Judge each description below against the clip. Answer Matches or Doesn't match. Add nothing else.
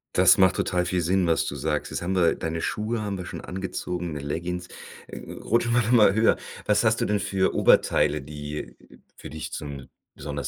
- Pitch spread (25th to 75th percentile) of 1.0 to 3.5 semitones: Doesn't match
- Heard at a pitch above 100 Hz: Doesn't match